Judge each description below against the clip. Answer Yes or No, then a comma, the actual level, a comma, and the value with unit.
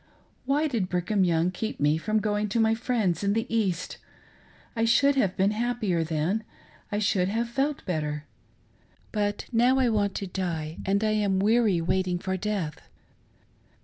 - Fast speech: No, average, 170 wpm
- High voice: Yes, high, 205 Hz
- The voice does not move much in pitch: No, average, 3.9 semitones